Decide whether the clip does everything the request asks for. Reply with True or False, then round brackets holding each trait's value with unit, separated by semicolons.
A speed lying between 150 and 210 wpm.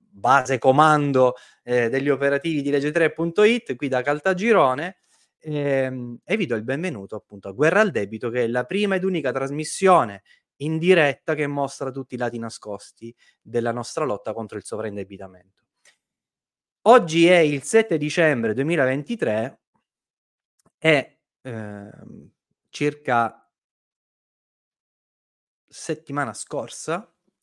False (115 wpm)